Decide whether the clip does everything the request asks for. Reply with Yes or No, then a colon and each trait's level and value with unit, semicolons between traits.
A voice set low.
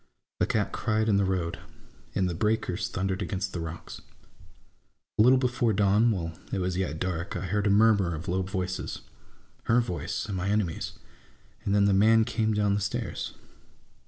Yes: low, 100 Hz